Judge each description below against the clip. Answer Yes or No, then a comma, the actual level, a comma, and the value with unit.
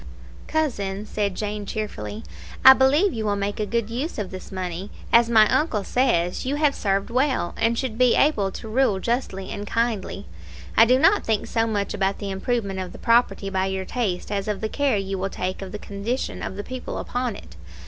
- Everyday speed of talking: No, fast, 210 wpm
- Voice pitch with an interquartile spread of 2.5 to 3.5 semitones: No, average, 4.0 semitones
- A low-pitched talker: No, high, 210 Hz